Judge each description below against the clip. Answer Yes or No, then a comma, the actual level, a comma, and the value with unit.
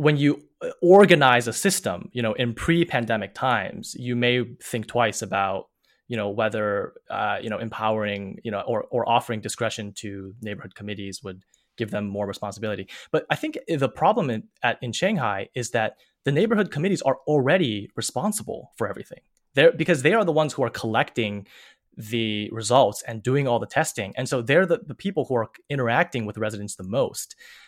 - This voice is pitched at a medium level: No, low, 120 Hz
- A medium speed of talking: Yes, average, 185 wpm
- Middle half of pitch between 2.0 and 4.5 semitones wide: No, wide, 5.5 semitones